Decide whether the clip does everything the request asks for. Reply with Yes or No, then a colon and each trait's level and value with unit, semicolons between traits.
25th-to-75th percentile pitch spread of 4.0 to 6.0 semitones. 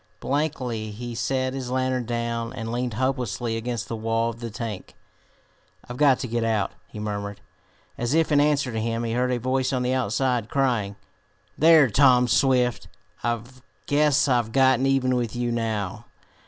No: narrow, 2.4 semitones